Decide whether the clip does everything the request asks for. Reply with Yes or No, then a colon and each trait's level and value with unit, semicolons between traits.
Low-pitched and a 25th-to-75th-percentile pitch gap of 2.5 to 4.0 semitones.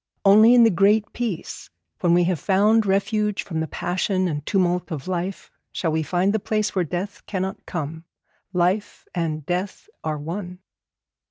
No: medium, 185 Hz; average, 3.1 semitones